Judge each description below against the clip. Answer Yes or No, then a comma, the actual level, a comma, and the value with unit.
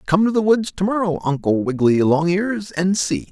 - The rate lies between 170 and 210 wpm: Yes, average, 200 wpm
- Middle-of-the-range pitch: Yes, medium, 180 Hz